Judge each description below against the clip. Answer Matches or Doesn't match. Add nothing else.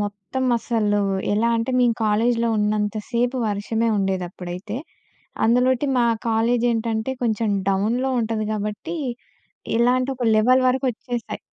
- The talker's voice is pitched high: Matches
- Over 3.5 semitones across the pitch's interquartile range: Doesn't match